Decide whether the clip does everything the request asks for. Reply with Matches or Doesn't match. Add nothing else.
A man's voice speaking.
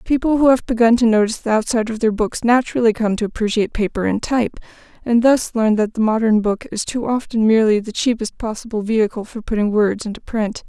Doesn't match